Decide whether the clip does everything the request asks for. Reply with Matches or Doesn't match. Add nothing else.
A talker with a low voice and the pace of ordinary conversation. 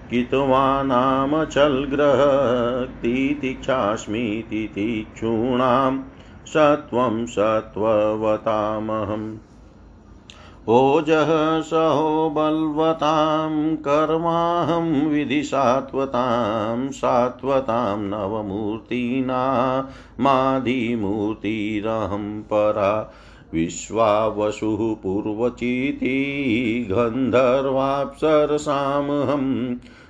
Doesn't match